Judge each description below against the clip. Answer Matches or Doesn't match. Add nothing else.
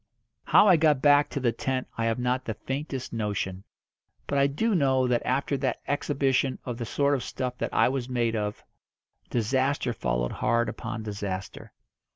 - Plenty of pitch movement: Doesn't match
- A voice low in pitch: Matches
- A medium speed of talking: Matches